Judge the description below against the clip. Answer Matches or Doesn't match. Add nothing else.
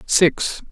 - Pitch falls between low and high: Matches